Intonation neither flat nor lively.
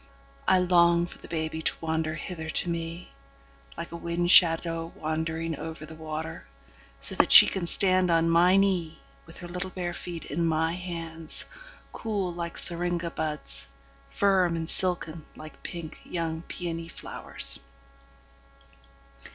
No: narrow, 1.8 semitones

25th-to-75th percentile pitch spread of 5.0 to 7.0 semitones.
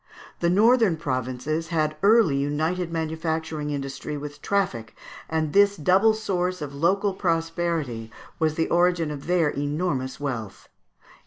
No: average, 3.7 semitones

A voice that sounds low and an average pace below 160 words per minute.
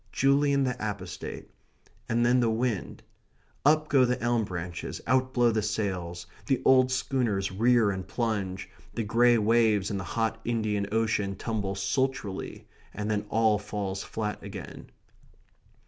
Yes: low, 110 Hz; average, 145 wpm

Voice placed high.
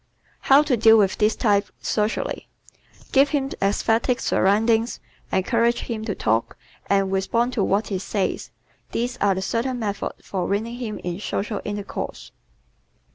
Yes: high, 215 Hz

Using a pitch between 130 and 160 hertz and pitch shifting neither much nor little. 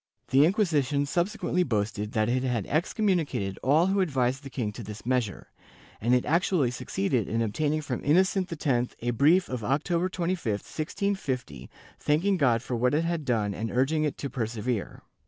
No: low, 135 Hz; wide, 6.0 semitones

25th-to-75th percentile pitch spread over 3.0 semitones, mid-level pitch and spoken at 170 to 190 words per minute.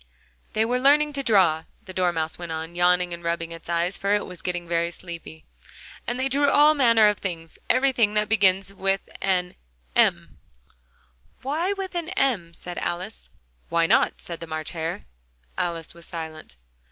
Yes: average, 5.2 semitones; medium, 180 Hz; average, 175 wpm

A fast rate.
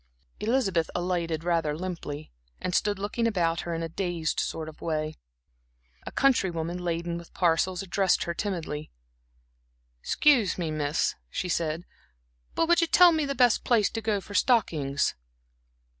No: average, 155 wpm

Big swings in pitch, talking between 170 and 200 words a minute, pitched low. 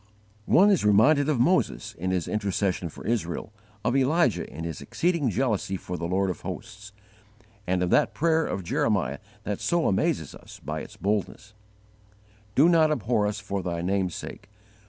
Yes: wide, 6.4 semitones; average, 175 wpm; low, 105 Hz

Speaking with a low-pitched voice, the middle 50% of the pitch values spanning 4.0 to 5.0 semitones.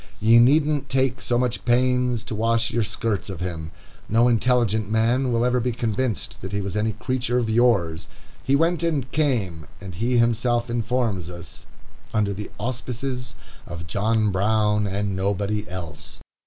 No: low, 115 Hz; average, 3.5 semitones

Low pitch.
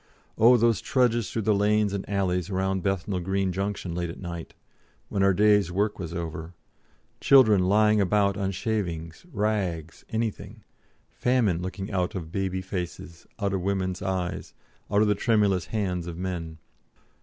Yes: very low, 95 Hz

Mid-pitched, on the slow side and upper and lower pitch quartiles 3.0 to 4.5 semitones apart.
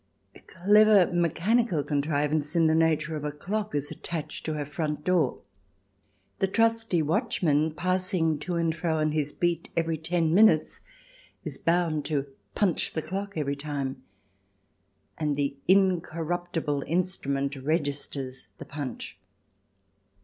Yes: medium, 160 Hz; slow, 130 wpm; average, 3.3 semitones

